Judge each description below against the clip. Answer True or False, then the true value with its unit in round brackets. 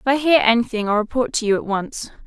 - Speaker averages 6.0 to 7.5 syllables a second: True (6.2 syllables/s)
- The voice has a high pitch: True (230 Hz)